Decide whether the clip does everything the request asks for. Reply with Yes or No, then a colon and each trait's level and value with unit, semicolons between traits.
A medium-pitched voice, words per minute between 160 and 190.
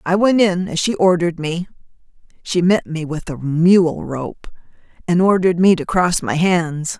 Yes: medium, 175 Hz; average, 180 wpm